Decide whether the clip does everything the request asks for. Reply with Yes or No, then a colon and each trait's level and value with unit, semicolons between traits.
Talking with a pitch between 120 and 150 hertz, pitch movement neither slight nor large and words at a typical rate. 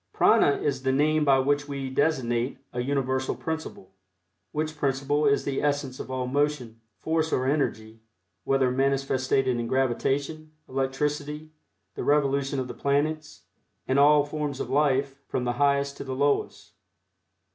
No: medium, 140 Hz; narrow, 1.9 semitones; average, 145 wpm